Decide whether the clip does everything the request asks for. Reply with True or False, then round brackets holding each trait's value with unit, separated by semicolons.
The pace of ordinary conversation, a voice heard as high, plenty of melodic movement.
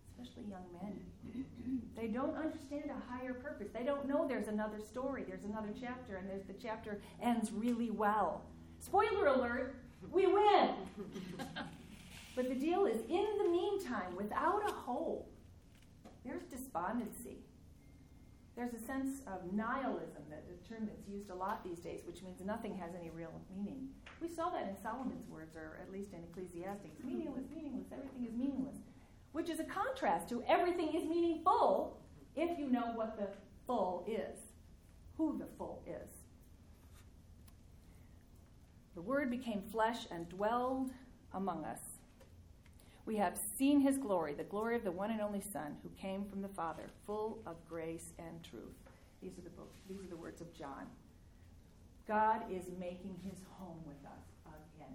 True (160 wpm; 220 Hz; 6.3 semitones)